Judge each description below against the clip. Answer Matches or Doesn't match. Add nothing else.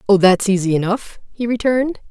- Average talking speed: Matches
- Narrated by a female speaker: Matches